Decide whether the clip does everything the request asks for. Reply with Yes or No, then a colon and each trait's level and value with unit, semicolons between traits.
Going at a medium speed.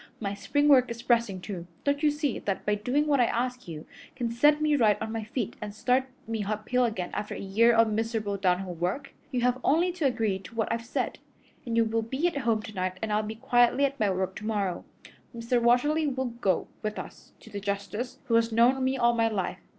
No: fast, 230 wpm